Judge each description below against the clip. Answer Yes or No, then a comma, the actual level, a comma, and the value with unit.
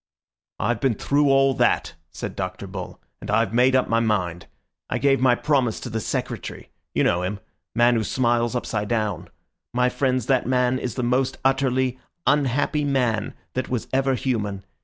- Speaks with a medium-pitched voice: No, low, 125 Hz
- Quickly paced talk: No, average, 170 wpm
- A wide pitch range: No, average, 2.7 semitones